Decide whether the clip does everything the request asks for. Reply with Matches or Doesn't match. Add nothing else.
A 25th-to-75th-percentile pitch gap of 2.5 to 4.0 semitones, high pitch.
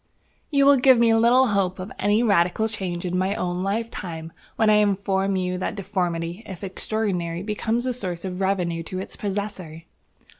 Matches